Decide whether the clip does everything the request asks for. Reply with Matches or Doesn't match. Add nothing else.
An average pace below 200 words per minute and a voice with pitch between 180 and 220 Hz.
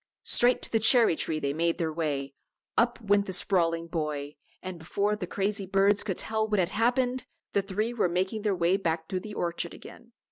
Doesn't match